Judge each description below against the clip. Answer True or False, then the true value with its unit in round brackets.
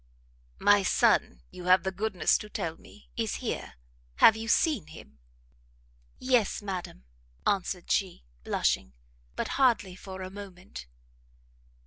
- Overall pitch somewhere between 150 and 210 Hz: True (190 Hz)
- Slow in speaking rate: True (125 wpm)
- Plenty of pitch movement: False (3.3 semitones)